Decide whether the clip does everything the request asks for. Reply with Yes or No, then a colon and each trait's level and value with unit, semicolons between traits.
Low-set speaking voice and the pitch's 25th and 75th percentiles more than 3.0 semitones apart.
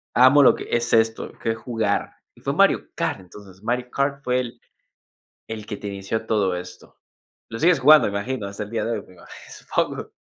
Yes: low, 110 Hz; average, 3.7 semitones